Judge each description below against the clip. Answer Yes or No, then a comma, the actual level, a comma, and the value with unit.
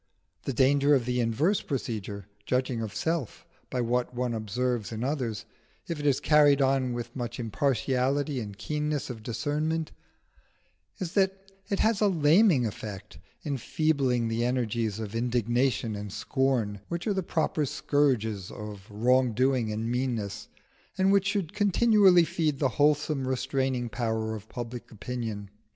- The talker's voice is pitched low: Yes, low, 125 Hz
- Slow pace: No, average, 145 wpm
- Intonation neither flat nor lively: Yes, average, 4.7 semitones